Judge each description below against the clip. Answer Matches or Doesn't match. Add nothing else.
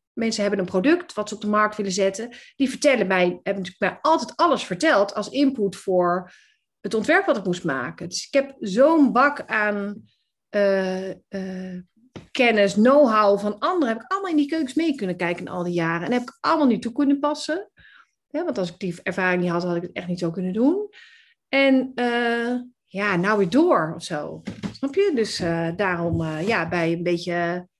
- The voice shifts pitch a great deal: Matches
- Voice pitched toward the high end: Matches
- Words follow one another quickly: Matches